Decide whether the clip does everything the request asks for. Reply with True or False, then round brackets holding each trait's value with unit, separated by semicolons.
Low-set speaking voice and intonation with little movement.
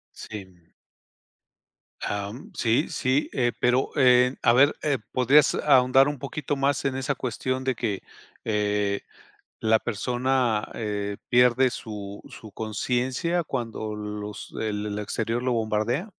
False (120 Hz; 3.8 semitones)